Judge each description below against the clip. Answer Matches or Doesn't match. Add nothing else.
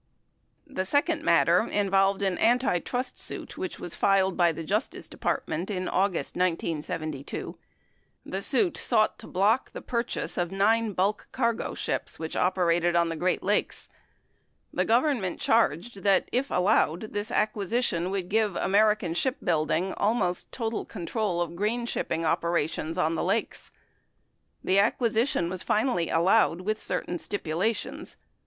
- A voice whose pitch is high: Matches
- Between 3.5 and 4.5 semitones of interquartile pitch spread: Matches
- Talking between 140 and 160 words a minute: Matches